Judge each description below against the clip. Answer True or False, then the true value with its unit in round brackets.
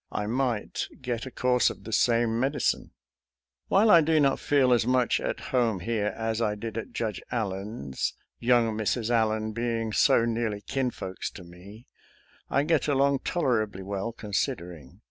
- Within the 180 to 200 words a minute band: True (185 wpm)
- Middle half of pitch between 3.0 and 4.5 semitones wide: True (3.3 semitones)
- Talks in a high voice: False (115 Hz)